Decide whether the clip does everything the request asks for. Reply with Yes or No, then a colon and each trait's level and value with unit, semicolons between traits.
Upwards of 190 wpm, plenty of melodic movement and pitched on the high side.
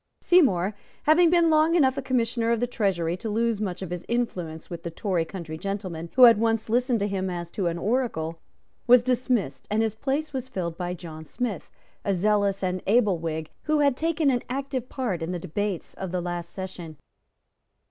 Yes: average, 200 wpm; wide, 6.1 semitones; high, 205 Hz